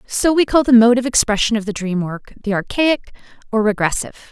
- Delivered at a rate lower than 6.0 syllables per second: No, 6.3 syllables/s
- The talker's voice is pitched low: No, high, 230 Hz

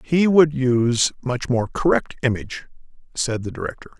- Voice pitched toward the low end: Yes, low, 130 Hz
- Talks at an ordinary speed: Yes, average, 150 wpm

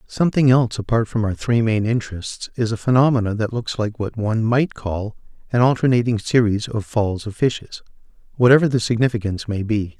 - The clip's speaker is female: No, male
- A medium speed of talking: Yes, average, 180 wpm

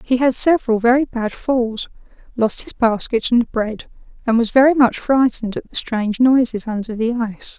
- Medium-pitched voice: No, high, 240 Hz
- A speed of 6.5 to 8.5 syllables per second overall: No, 5.1 syllables/s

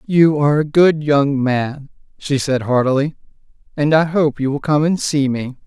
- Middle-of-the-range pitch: Yes, medium, 145 Hz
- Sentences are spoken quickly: No, average, 190 wpm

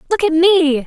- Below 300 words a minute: Yes, fast, 210 wpm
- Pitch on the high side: Yes, very high, 335 Hz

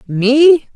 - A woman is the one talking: Yes, female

